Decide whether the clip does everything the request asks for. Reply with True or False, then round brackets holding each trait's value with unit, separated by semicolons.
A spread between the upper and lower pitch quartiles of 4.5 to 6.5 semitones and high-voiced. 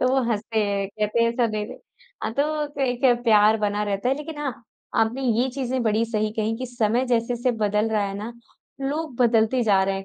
False (3.2 semitones; 230 Hz)